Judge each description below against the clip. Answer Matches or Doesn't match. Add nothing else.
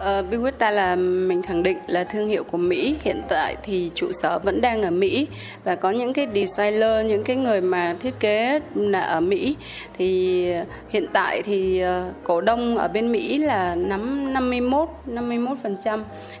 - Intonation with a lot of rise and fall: Matches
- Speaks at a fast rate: Doesn't match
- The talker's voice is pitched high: Matches